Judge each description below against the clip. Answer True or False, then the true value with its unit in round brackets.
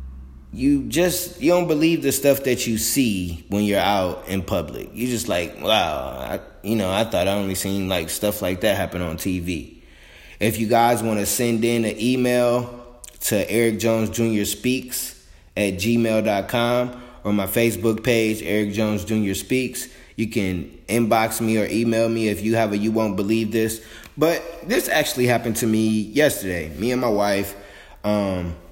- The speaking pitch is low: True (110 Hz)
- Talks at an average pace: True (180 wpm)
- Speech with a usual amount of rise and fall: True (3.2 semitones)